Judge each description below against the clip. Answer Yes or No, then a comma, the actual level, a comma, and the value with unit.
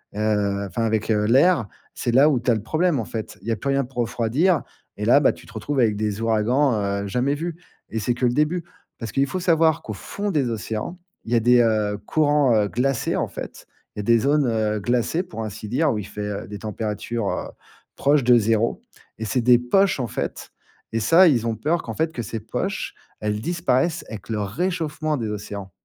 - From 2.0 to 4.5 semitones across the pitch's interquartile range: No, wide, 5.5 semitones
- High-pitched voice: No, low, 120 Hz